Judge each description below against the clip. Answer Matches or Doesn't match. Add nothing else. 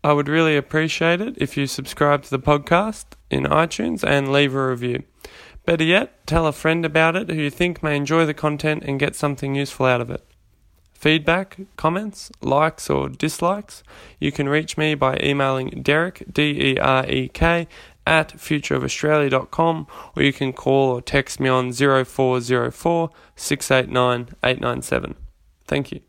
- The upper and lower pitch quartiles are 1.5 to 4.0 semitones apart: Matches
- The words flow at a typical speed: Matches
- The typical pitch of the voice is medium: Matches